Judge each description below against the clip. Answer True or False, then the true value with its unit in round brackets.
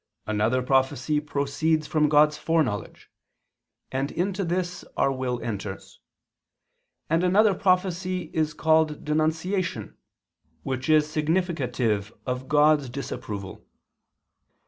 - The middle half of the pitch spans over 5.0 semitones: False (4.2 semitones)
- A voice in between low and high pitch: True (150 Hz)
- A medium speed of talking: False (100 wpm)